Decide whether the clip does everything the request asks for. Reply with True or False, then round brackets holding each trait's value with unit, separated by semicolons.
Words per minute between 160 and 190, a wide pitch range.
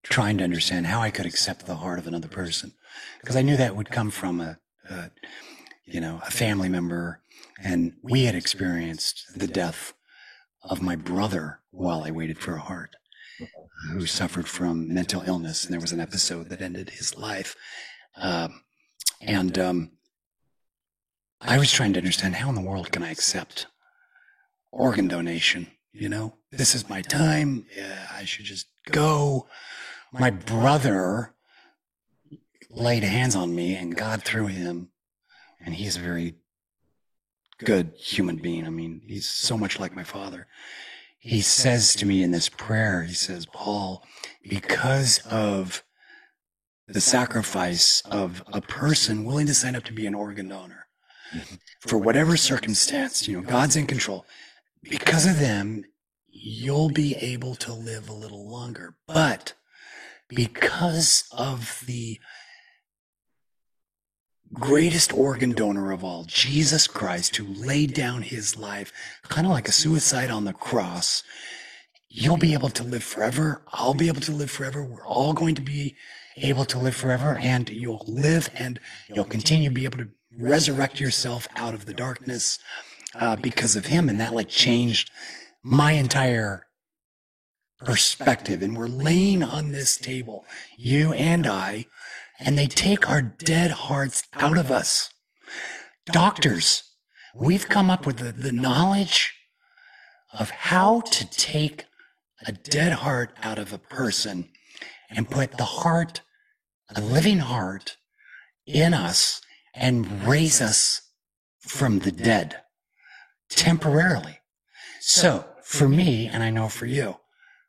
False (145 wpm; 6.3 semitones)